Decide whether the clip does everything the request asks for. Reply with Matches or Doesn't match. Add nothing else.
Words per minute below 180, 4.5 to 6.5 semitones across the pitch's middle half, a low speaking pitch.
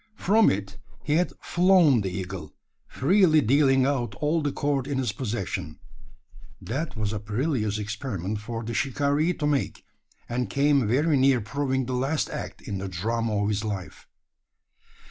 Matches